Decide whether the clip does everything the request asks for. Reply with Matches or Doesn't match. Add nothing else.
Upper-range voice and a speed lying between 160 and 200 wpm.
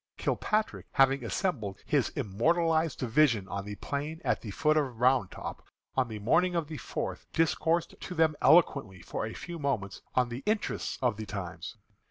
Doesn't match